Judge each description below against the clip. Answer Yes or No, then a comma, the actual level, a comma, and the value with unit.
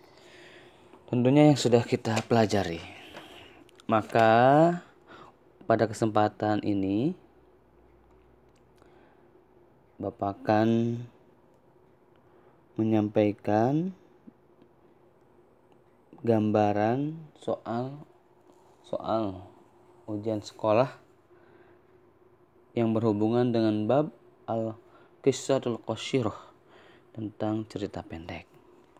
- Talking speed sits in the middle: No, slow, 50 wpm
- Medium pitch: No, low, 115 Hz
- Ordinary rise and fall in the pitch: Yes, average, 3.2 semitones